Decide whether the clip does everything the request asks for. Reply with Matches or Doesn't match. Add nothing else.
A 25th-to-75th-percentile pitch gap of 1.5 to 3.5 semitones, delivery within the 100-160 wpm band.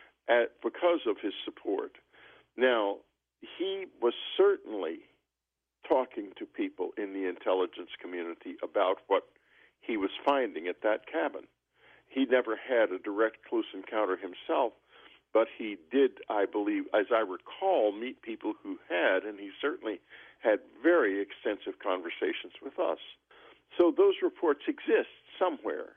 Doesn't match